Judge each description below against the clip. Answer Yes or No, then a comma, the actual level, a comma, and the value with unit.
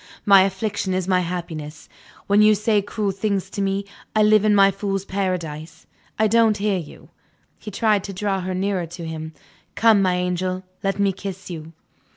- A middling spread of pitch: No, narrow, 2.2 semitones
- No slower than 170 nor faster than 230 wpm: Yes, average, 185 wpm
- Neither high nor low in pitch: No, high, 195 Hz